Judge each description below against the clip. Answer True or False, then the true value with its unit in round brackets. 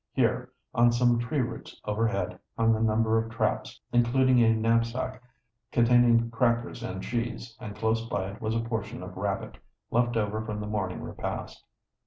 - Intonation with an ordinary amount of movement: False (1.6 semitones)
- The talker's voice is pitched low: True (115 Hz)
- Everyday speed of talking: True (165 wpm)